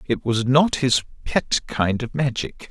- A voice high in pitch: No, low, 130 Hz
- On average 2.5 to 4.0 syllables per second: Yes, 3.8 syllables/s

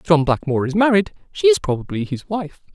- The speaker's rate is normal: No, fast, 220 wpm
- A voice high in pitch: No, medium, 170 Hz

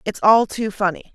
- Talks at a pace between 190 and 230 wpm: Yes, fast, 210 wpm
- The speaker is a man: No, female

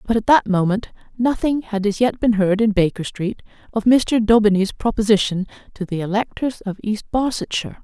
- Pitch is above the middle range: Yes, high, 215 Hz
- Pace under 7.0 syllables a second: Yes, 5.3 syllables/s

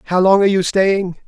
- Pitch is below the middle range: No, high, 190 Hz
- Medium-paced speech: No, fast, 235 wpm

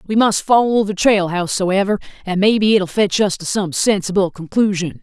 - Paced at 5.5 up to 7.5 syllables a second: No, 5.0 syllables/s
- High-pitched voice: Yes, high, 200 Hz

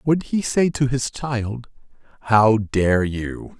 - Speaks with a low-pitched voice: Yes, low, 120 Hz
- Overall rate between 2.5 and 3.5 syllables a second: Yes, 3.0 syllables/s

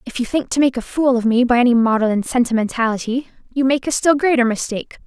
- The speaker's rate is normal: No, fast, 225 wpm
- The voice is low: No, very high, 250 Hz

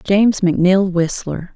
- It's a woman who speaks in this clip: Yes, female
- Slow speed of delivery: Yes, slow, 115 wpm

